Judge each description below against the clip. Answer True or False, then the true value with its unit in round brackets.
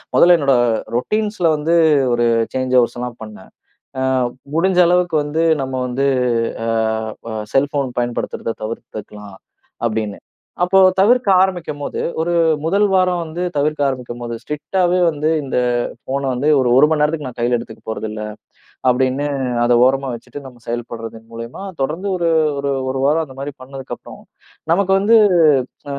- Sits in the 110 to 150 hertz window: True (140 Hz)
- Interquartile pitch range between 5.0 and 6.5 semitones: True (5.5 semitones)